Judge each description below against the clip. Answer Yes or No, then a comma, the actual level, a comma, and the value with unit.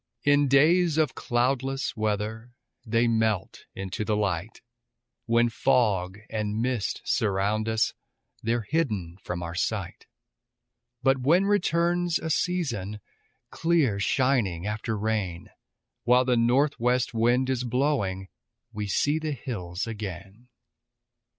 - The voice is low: Yes, low, 115 Hz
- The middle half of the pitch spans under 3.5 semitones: No, average, 4.6 semitones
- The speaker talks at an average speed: No, slow, 115 wpm